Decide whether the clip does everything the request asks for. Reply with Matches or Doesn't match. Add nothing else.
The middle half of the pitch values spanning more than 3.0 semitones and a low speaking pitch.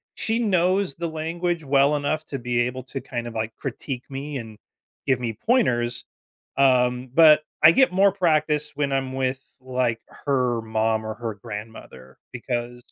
Matches